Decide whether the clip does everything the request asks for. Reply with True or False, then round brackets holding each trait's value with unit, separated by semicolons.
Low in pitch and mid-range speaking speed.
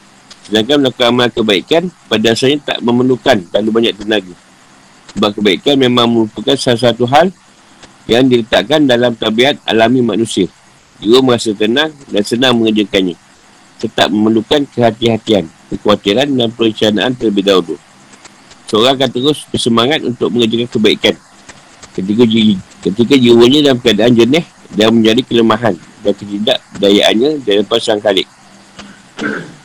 True (115 Hz; 115 wpm)